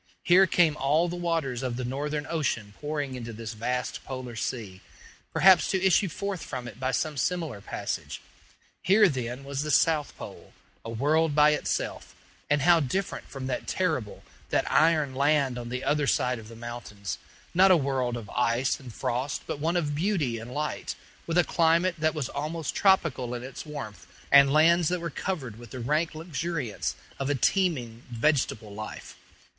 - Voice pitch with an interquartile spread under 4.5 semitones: No, average, 5.0 semitones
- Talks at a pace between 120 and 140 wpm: No, average, 180 wpm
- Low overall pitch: No, medium, 145 Hz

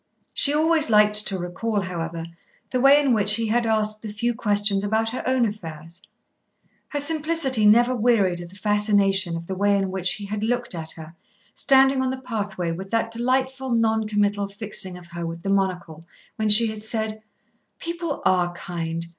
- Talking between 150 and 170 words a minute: No, average, 185 wpm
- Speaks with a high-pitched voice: Yes, high, 210 Hz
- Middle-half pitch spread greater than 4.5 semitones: No, average, 4.2 semitones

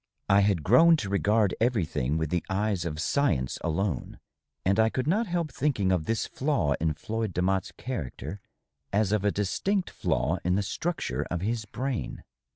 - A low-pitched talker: Yes, low, 100 Hz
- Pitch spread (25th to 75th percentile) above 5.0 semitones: Yes, wide, 5.4 semitones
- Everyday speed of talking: Yes, average, 170 wpm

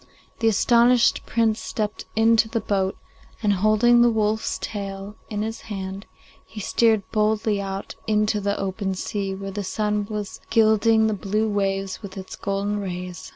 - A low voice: No, high, 210 Hz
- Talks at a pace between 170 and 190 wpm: No, average, 155 wpm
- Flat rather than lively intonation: Yes, narrow, 2.0 semitones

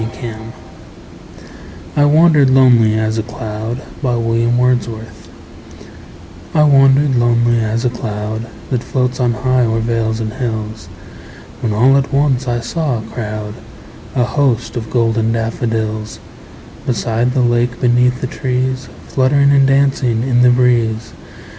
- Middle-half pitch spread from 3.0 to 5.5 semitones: No, narrow, 2.4 semitones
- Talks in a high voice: No, low, 120 Hz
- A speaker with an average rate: No, slow, 130 wpm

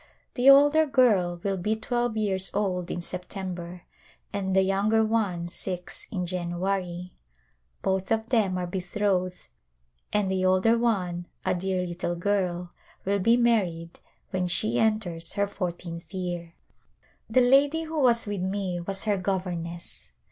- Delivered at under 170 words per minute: Yes, average, 140 wpm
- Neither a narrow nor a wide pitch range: Yes, average, 3.4 semitones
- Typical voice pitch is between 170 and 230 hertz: Yes, high, 190 Hz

